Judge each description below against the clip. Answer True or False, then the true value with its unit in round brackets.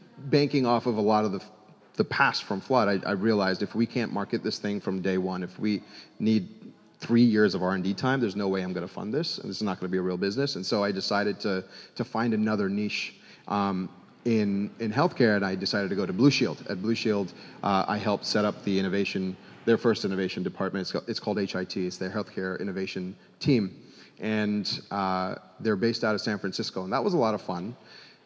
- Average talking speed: False (230 wpm)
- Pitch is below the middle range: True (100 Hz)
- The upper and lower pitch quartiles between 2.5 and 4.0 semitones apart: True (2.9 semitones)